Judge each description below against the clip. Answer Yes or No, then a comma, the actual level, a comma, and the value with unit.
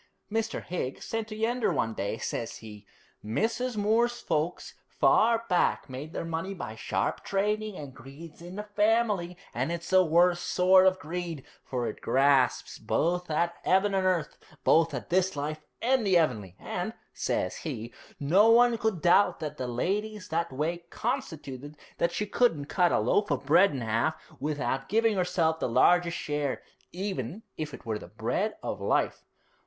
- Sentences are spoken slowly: No, average, 170 wpm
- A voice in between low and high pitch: Yes, medium, 170 Hz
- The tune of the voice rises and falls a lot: Yes, wide, 6.4 semitones